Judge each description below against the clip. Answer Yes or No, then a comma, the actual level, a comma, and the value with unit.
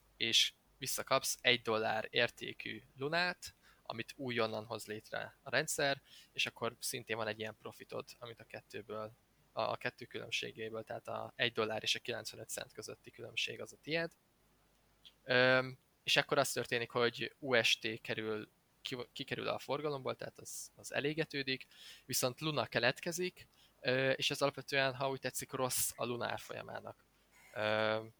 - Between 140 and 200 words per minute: Yes, average, 145 wpm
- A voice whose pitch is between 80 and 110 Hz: No, low, 125 Hz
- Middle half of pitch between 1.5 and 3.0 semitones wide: No, average, 3.7 semitones